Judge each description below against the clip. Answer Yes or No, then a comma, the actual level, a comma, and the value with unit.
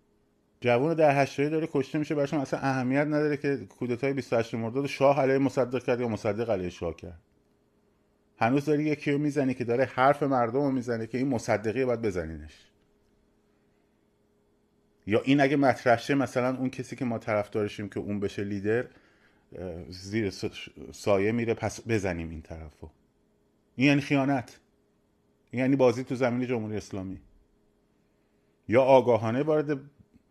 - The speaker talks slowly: No, average, 150 wpm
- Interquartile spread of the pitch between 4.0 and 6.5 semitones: Yes, average, 4.9 semitones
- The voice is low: Yes, low, 125 Hz